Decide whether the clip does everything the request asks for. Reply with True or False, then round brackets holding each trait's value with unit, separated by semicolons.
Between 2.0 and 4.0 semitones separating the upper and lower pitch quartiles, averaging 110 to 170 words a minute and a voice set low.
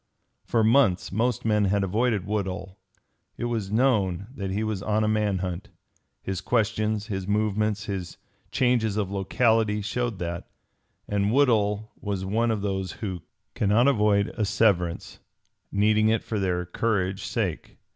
True (2.4 semitones; 145 wpm; 105 Hz)